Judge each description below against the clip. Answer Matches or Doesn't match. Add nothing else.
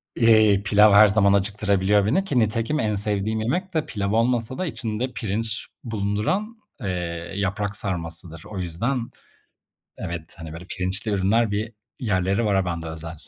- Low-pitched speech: Matches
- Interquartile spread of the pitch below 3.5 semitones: Matches